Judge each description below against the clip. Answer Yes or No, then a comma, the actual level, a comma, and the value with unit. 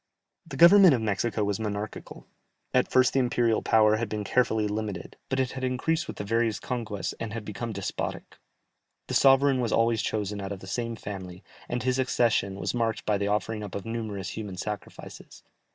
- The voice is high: No, low, 110 Hz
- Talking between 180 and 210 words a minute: Yes, average, 190 wpm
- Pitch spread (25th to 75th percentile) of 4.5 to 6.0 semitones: No, average, 3.1 semitones